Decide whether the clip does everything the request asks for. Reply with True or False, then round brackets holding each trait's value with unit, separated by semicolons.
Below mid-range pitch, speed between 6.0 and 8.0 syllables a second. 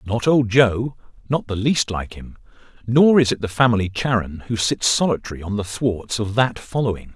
False (110 Hz; 5.0 syllables/s)